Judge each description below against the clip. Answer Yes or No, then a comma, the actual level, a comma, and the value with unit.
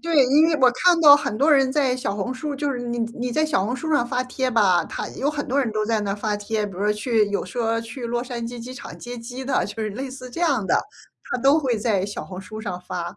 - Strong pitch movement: No, average, 4.2 semitones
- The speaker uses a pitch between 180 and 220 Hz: No, high, 245 Hz